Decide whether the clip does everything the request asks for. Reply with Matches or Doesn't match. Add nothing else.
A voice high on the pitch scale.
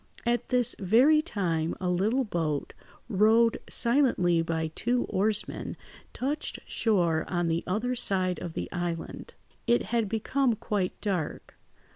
Matches